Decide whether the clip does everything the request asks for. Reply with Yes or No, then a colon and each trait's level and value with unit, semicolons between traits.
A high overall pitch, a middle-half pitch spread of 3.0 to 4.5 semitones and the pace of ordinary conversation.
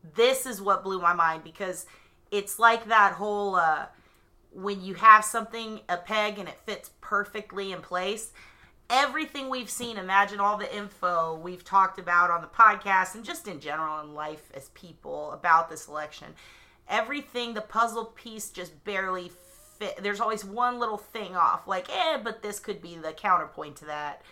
Yes: high, 200 Hz; average, 4.0 semitones; average, 175 wpm